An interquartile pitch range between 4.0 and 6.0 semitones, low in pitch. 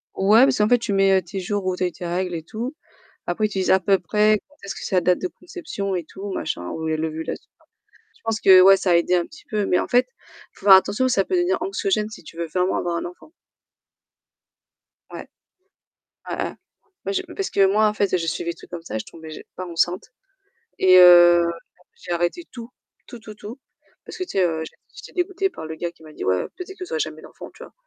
No: average, 4.4 semitones; high, 190 Hz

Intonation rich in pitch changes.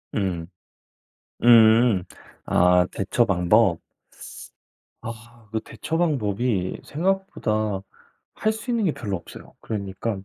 No: average, 4.4 semitones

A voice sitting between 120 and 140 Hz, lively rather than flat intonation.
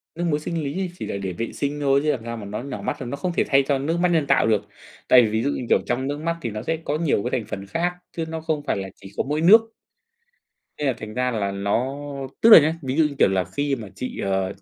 Yes: low, 135 Hz; wide, 6.4 semitones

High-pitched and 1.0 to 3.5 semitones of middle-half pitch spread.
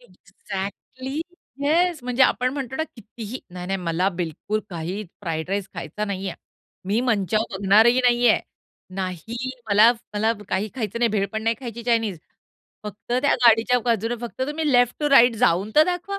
No: high, 225 Hz; average, 4.2 semitones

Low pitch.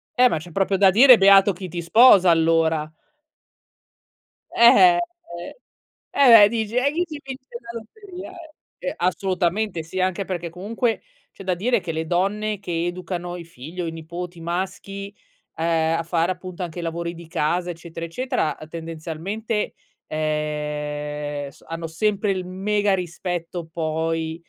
No: medium, 180 Hz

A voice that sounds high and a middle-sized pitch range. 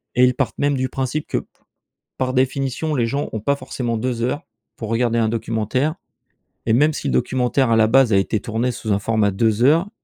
No: low, 125 Hz; average, 3.1 semitones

